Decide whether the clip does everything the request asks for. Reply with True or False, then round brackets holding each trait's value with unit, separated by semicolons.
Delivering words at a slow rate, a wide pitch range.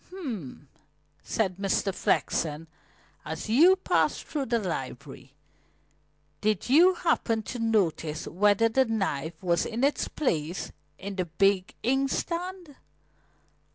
True (115 wpm; 8.0 semitones)